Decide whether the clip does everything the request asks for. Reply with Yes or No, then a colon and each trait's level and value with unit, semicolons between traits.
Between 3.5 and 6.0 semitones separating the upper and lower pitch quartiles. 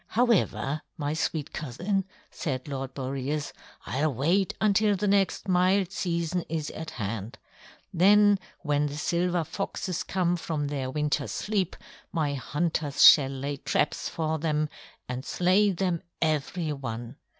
Yes: average, 4.5 semitones